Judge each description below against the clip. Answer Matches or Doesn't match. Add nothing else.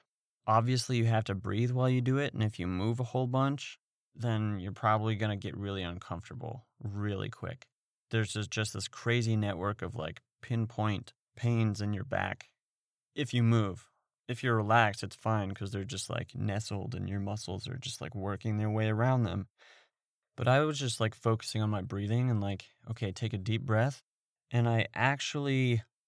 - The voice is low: Matches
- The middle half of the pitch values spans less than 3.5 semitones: Matches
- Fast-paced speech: Doesn't match